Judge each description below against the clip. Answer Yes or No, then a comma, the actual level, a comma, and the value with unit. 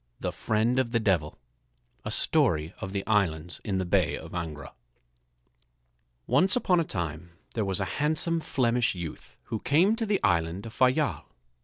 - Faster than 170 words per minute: No, average, 165 wpm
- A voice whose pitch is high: No, low, 110 Hz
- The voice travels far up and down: Yes, wide, 8.2 semitones